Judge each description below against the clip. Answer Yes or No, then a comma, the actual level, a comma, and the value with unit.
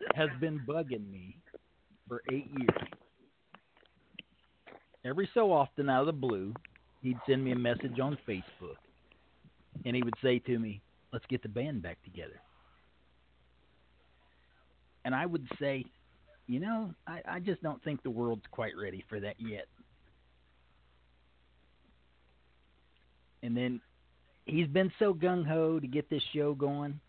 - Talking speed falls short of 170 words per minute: Yes, average, 140 wpm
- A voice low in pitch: Yes, low, 120 Hz